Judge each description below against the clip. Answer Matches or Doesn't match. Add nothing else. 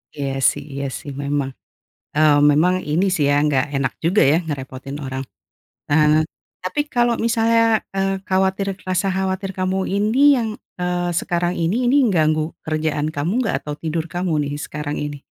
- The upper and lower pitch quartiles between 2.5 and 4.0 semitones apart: Doesn't match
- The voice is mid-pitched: Matches